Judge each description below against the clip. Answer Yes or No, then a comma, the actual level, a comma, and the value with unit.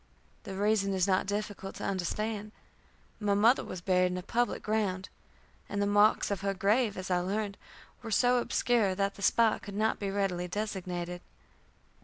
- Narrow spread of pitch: Yes, narrow, 2.3 semitones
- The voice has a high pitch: Yes, high, 200 Hz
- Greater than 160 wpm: Yes, average, 175 wpm